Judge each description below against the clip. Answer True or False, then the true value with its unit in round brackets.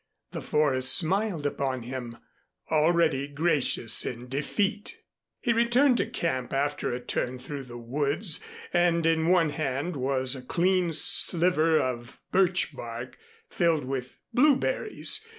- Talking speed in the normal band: False (130 wpm)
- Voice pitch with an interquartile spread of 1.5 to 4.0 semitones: False (5.4 semitones)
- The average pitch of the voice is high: False (150 Hz)